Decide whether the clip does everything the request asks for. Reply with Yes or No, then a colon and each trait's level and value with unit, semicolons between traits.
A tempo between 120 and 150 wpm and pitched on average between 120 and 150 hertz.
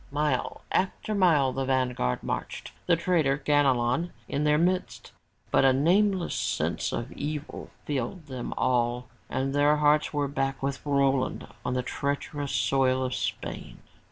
Yes: average, 145 wpm; medium, 140 Hz